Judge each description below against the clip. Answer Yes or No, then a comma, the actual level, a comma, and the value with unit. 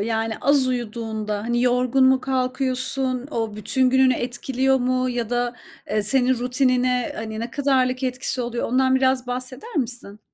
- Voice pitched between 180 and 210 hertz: No, very high, 250 Hz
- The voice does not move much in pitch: Yes, narrow, 1.6 semitones